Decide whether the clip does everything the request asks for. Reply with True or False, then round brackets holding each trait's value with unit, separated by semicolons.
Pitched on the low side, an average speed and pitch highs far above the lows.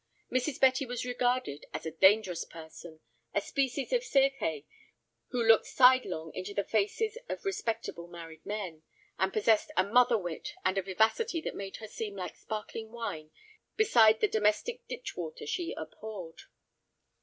False (220 Hz; 155 wpm; 5.7 semitones)